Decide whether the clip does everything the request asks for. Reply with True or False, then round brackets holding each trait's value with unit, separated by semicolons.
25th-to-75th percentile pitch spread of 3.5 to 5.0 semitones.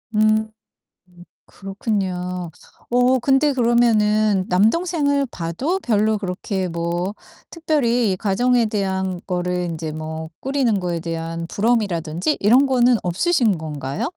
False (5.4 semitones)